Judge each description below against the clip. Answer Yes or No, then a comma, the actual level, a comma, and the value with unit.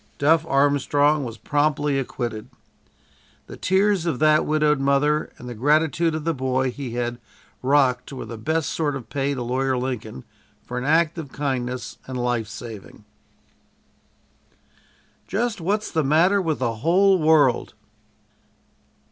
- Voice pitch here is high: No, medium, 140 Hz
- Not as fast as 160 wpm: Yes, average, 140 wpm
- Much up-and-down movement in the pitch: No, average, 4.0 semitones